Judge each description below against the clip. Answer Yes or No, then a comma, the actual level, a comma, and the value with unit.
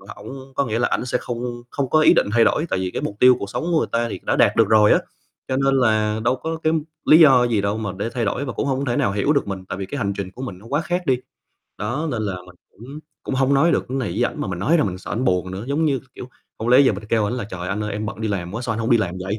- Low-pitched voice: Yes, low, 115 Hz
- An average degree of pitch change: Yes, average, 4.9 semitones